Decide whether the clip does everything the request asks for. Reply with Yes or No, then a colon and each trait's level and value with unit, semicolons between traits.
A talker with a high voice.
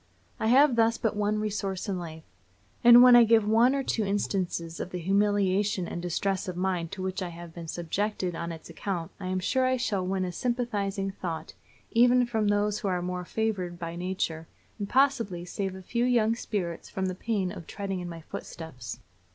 Yes: high, 195 Hz